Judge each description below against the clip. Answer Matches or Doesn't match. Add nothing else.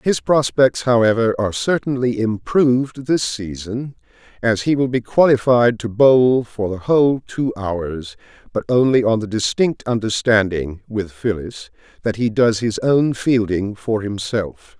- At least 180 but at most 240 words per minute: Doesn't match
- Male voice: Matches